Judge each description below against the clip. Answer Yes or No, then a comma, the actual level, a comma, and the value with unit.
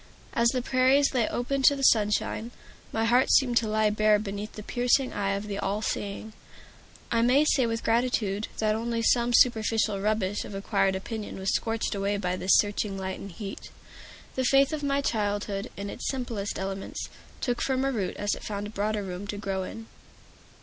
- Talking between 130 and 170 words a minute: No, average, 185 wpm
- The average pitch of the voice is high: Yes, high, 215 Hz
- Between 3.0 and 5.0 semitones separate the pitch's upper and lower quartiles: Yes, average, 3.3 semitones